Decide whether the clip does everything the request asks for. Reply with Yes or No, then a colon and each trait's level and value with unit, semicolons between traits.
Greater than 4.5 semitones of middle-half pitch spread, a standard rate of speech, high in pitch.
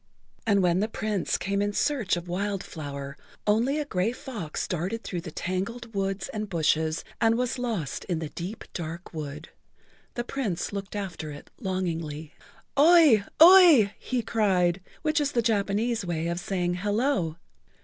Yes: average, 5.0 semitones; average, 160 wpm; high, 195 Hz